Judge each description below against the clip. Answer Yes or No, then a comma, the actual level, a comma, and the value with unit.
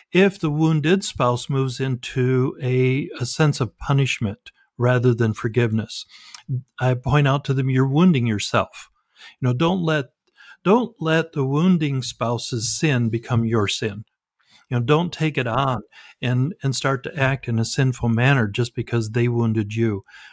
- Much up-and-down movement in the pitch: No, average, 3.9 semitones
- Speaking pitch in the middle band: No, low, 130 Hz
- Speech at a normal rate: Yes, average, 160 wpm